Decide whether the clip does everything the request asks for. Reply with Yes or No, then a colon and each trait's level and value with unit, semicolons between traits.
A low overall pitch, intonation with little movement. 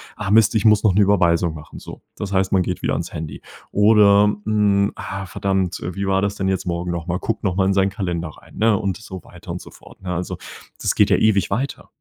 Yes: very low, 95 Hz; narrow, 2.2 semitones